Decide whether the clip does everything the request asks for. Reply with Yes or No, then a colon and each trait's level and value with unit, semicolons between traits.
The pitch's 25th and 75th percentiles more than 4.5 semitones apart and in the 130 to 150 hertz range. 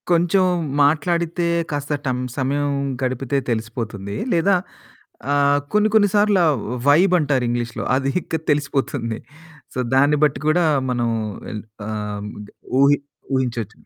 Yes: average, 5.3 semitones; medium, 140 Hz